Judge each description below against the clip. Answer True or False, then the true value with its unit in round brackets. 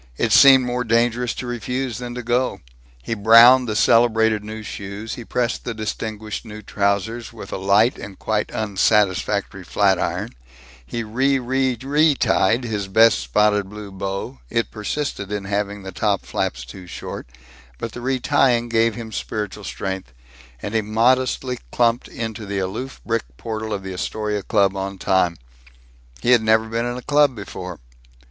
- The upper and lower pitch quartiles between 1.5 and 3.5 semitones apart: True (3.2 semitones)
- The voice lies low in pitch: True (110 Hz)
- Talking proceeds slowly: False (160 wpm)